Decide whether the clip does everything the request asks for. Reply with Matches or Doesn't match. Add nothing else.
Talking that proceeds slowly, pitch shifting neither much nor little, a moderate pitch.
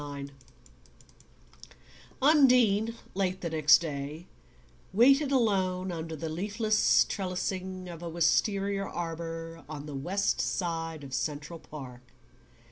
Matches